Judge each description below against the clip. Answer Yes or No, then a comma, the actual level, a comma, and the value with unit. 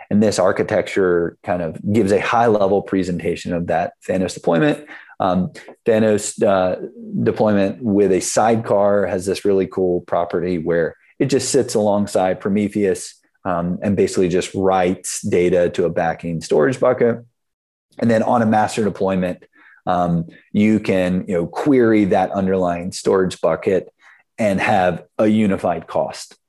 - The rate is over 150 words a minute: No, average, 145 wpm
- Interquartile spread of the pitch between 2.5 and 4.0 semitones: Yes, average, 3.0 semitones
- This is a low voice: Yes, very low, 95 Hz